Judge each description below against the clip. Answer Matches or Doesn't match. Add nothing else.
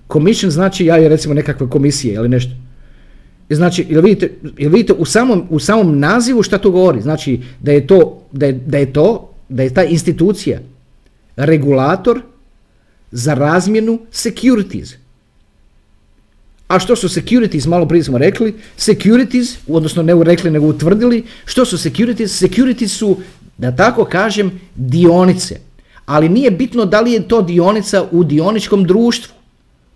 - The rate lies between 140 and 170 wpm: Matches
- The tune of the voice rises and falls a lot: Matches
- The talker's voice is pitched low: Doesn't match